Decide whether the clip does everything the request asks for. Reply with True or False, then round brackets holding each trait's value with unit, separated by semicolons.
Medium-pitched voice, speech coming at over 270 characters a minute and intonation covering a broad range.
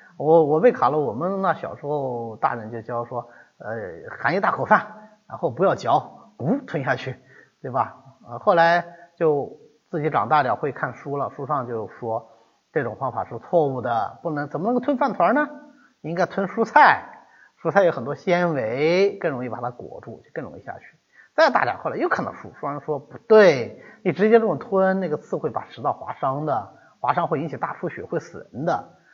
True (170 Hz; 280 characters per minute; 7.3 semitones)